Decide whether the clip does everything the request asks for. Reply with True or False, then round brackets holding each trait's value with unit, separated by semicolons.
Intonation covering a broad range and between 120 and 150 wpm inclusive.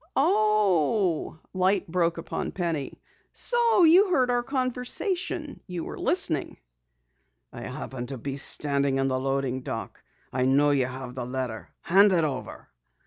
True (8.3 semitones; 140 wpm)